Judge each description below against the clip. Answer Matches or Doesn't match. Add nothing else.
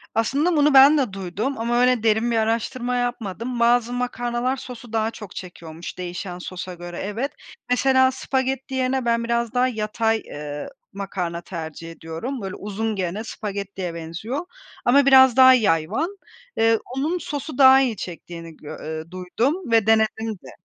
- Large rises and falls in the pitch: Matches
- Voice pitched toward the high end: Matches